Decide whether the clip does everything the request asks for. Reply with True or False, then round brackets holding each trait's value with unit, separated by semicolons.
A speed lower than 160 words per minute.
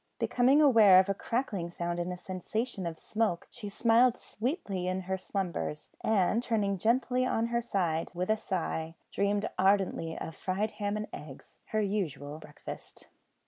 False (165 wpm)